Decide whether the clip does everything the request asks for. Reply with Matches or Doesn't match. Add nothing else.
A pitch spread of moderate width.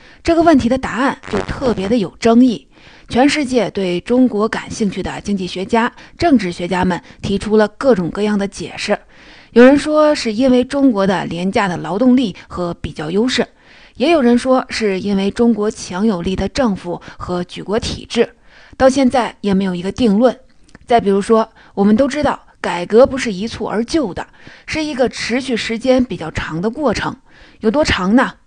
Matches